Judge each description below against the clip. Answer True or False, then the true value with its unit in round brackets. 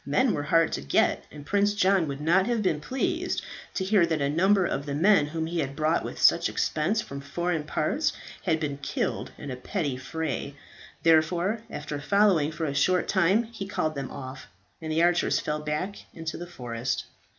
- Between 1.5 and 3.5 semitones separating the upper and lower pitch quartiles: False (4.7 semitones)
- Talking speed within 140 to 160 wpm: False (195 wpm)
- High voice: False (160 Hz)